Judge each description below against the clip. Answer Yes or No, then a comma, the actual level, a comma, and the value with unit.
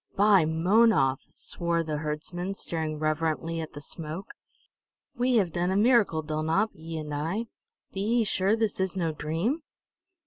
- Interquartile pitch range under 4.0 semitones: No, average, 4.6 semitones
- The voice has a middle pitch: Yes, medium, 170 Hz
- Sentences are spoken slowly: No, average, 150 wpm